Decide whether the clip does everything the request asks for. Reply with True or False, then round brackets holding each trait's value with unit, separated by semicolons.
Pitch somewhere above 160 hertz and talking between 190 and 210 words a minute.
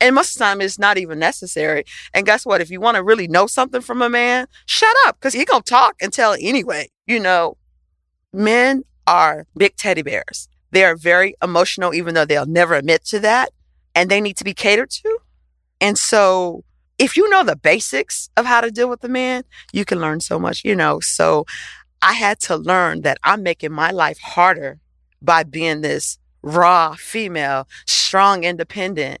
True (190 Hz; 200 wpm)